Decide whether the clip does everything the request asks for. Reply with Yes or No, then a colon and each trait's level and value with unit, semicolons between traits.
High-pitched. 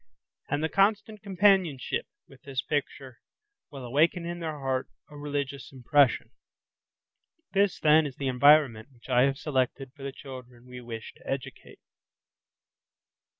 No: medium, 140 Hz